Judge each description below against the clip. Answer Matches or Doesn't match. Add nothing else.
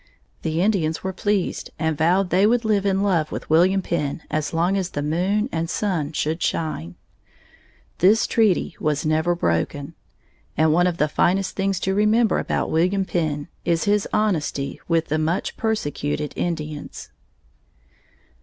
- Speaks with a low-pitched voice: Doesn't match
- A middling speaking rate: Matches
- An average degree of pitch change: Matches